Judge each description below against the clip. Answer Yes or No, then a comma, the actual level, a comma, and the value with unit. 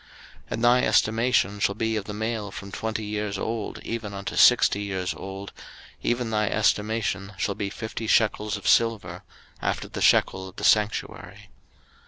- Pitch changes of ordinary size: No, narrow, 2.0 semitones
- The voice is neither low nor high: No, low, 105 Hz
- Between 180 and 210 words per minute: No, average, 165 wpm